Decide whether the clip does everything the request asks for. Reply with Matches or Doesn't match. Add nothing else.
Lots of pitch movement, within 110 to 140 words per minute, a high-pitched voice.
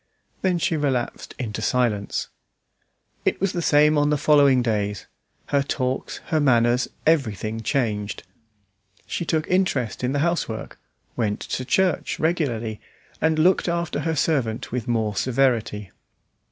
Doesn't match